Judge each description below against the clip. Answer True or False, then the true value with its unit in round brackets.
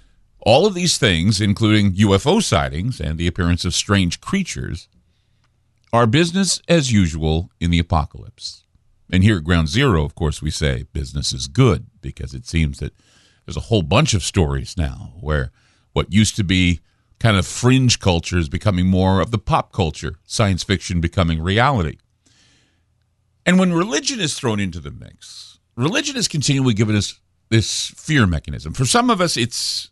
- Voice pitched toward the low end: True (100 Hz)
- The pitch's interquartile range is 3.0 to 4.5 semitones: False (5.5 semitones)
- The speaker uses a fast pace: False (170 wpm)